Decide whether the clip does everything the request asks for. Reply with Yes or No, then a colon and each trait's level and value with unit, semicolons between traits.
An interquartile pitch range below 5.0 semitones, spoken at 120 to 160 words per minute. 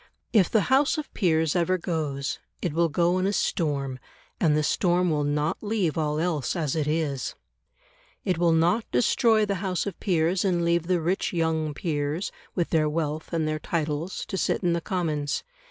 No: average, 3.1 semitones; average, 185 wpm